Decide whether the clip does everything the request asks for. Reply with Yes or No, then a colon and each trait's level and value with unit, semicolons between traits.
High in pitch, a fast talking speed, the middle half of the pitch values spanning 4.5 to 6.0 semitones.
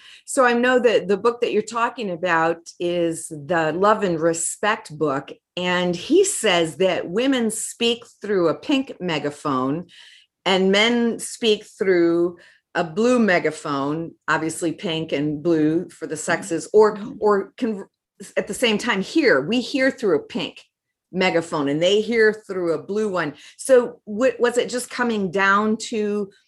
No: high, 195 Hz; average, 155 wpm; wide, 5.6 semitones